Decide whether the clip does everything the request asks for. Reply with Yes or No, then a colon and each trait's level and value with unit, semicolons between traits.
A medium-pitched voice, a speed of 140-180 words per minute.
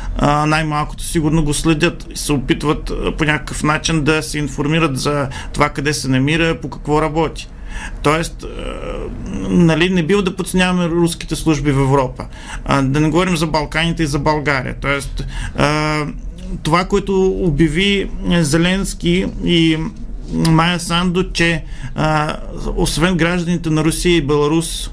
No: medium, 160 Hz; average, 130 wpm